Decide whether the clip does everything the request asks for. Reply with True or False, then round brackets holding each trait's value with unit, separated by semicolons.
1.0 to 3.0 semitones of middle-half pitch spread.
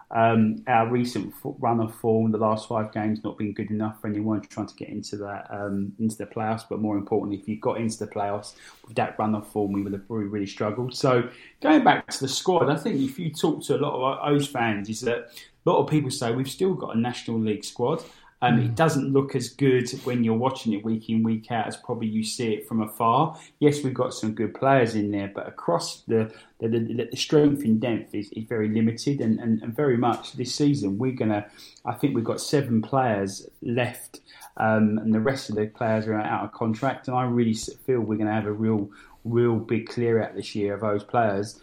True (2.6 semitones)